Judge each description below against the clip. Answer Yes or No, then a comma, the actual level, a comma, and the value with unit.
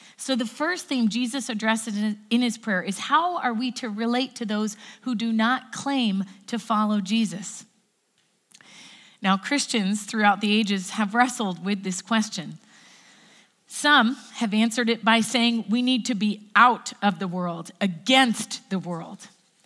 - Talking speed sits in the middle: Yes, average, 155 wpm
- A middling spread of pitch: Yes, average, 3.2 semitones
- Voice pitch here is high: Yes, high, 220 Hz